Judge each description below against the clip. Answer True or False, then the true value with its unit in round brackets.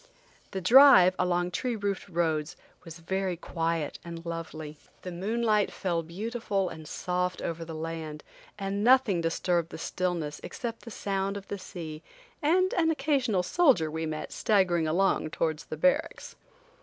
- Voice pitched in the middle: True (180 Hz)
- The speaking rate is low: False (150 wpm)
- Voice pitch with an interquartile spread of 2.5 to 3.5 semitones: False (3.9 semitones)